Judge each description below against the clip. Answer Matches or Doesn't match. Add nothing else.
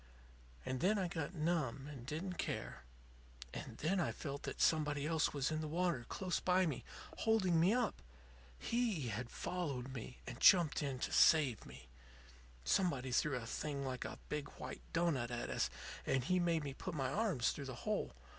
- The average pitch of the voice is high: Doesn't match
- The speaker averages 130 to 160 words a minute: Doesn't match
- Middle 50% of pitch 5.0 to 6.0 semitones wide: Matches